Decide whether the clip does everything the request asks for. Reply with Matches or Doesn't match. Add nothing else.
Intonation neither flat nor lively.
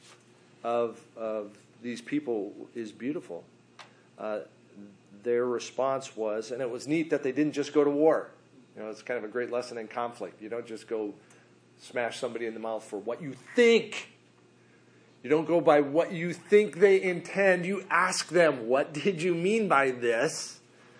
Doesn't match